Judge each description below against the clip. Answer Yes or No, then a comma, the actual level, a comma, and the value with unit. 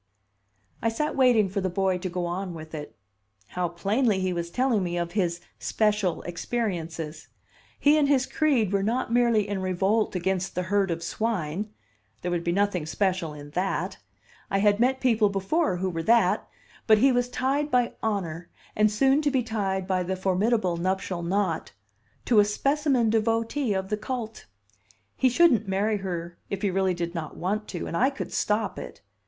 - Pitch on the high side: Yes, high, 200 Hz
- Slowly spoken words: No, average, 180 wpm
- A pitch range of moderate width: Yes, average, 4.3 semitones